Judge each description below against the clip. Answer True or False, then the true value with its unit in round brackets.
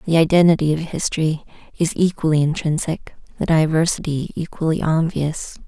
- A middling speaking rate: False (115 wpm)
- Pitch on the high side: False (160 Hz)